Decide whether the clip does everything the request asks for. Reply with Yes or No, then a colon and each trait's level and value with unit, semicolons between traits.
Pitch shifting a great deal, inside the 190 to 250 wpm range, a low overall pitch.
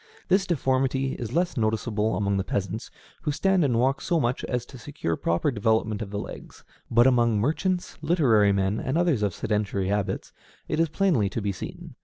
Yes: wide, 5.9 semitones; average, 195 wpm; low, 120 Hz